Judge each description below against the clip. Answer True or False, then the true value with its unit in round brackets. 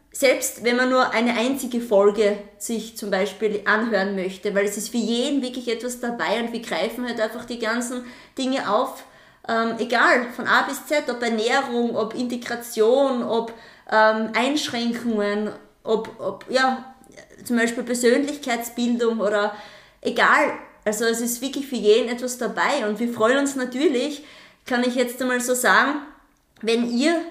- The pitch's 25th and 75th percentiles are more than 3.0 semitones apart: False (2.5 semitones)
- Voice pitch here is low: False (235 Hz)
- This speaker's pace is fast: False (155 wpm)